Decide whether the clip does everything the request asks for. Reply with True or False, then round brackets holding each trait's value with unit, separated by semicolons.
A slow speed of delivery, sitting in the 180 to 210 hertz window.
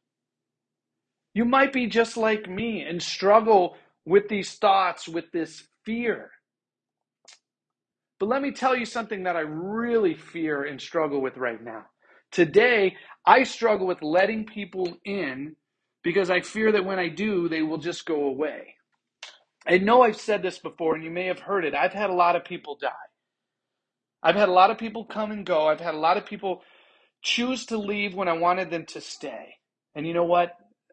False (185 wpm; 190 Hz)